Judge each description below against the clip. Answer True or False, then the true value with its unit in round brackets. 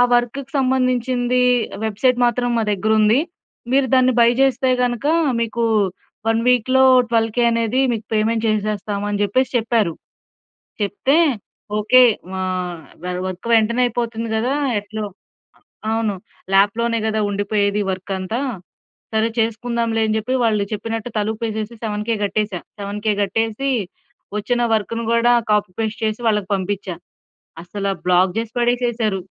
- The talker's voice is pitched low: False (225 Hz)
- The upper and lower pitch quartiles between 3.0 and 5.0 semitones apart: False (2.6 semitones)